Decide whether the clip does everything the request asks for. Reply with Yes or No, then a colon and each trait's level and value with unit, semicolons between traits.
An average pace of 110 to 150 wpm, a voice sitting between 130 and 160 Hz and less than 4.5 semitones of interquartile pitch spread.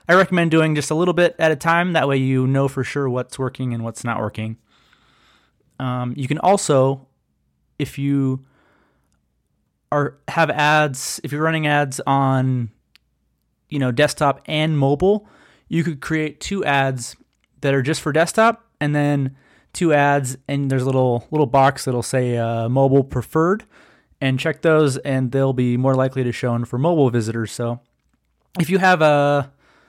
No: average, 170 wpm; medium, 140 Hz; average, 3.4 semitones